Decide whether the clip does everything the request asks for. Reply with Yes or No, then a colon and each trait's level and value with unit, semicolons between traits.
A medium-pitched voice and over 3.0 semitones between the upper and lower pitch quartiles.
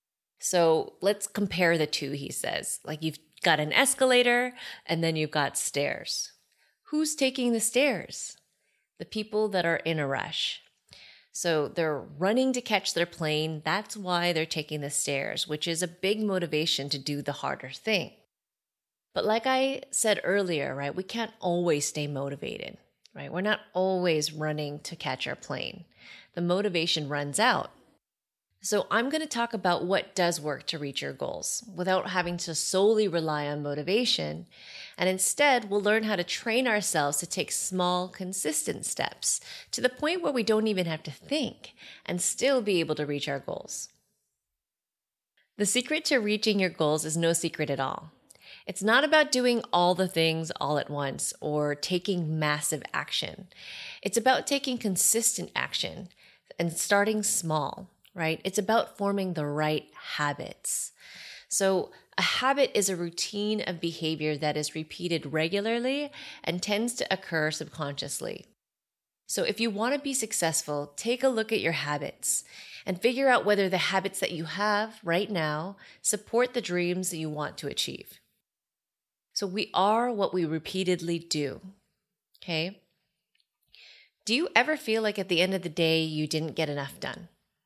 Yes: medium, 180 Hz; wide, 5.5 semitones